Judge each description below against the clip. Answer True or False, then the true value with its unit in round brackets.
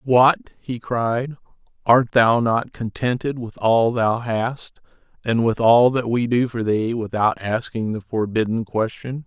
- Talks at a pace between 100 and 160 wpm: True (155 wpm)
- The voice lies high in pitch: False (115 Hz)